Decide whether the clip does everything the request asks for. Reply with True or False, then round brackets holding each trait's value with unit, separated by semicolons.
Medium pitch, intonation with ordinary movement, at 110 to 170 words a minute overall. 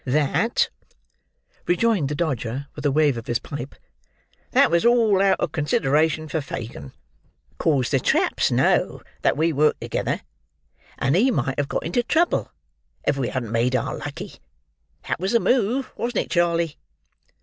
False (155 Hz; 5.9 semitones; 160 wpm)